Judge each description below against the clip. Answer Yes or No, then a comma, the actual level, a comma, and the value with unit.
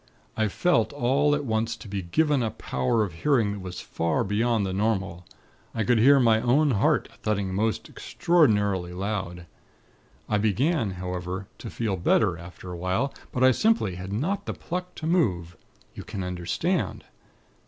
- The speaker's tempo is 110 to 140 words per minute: No, average, 165 wpm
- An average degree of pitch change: No, wide, 5.9 semitones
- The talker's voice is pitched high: No, low, 105 Hz